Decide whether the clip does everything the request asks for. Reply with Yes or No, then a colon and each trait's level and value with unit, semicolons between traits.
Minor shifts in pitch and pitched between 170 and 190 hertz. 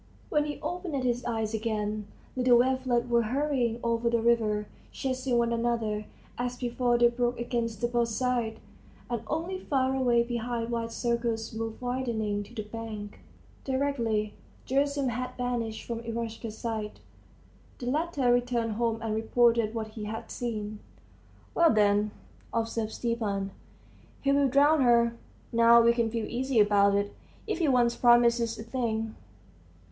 No: narrow, 1.9 semitones; high, 235 Hz